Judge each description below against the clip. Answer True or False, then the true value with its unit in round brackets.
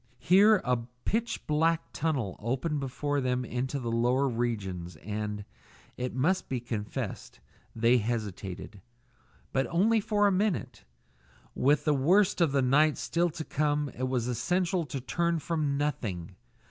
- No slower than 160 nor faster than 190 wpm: False (145 wpm)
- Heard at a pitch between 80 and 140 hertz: True (135 Hz)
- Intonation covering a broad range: True (5.7 semitones)